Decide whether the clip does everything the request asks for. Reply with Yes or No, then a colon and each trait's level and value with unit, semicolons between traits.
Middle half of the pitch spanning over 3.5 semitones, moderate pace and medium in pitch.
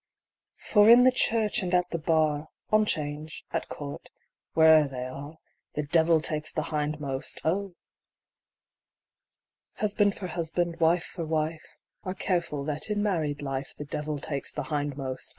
No: average, 3.2 semitones; average, 145 wpm; medium, 155 Hz